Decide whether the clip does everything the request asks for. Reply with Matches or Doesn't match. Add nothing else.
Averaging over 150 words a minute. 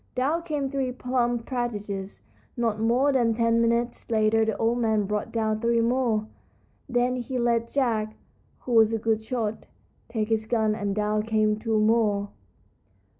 Matches